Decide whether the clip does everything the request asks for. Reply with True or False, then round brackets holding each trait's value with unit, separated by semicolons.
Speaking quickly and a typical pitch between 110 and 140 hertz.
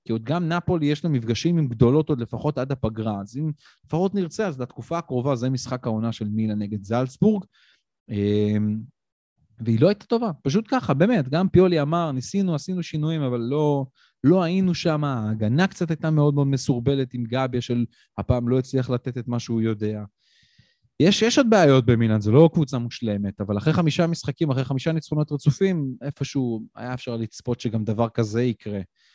True (180 wpm; 135 Hz)